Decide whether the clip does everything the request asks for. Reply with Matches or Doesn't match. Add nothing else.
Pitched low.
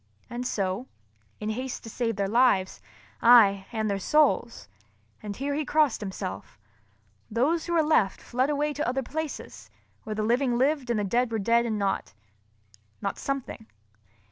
Doesn't match